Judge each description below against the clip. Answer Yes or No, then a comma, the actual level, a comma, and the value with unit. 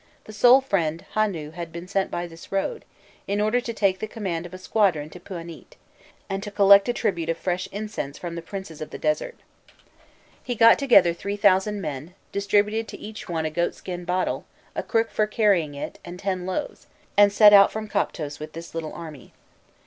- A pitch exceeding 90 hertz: Yes, high, 190 Hz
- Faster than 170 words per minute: Yes, average, 195 wpm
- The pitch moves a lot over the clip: No, average, 3.9 semitones